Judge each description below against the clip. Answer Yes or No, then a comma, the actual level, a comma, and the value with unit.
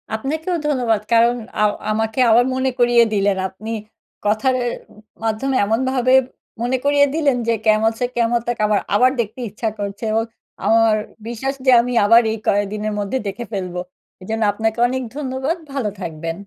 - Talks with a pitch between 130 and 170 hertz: No, high, 230 Hz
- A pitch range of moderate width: Yes, average, 3.4 semitones